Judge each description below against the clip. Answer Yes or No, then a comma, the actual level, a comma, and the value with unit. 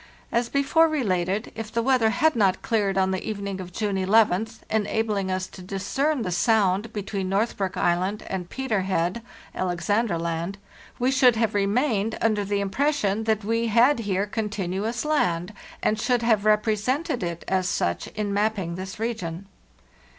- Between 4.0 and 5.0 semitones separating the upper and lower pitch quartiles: No, average, 3.3 semitones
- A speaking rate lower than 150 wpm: No, average, 165 wpm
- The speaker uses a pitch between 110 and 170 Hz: No, high, 210 Hz